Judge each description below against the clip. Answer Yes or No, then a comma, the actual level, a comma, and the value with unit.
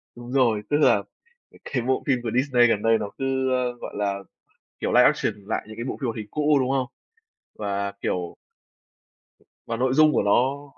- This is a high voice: No, low, 125 Hz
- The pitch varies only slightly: No, average, 3.4 semitones